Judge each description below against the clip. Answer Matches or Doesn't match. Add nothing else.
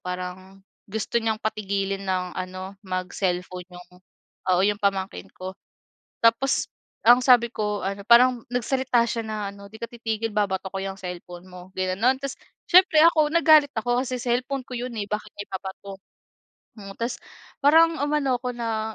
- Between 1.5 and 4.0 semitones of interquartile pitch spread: Doesn't match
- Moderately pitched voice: Doesn't match